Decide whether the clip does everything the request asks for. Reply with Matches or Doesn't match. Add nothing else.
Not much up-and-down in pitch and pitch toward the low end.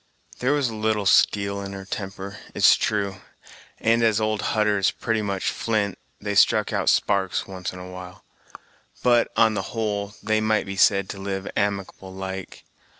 Matches